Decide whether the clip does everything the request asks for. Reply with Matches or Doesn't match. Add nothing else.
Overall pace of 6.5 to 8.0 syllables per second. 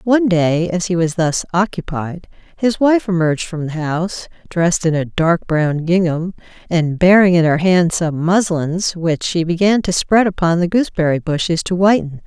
Doesn't match